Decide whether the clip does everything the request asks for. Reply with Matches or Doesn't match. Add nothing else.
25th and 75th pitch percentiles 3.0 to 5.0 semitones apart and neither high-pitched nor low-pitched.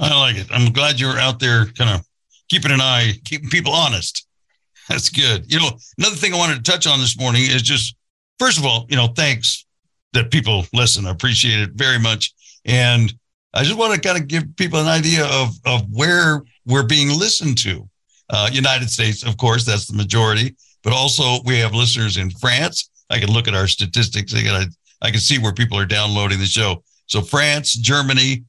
Doesn't match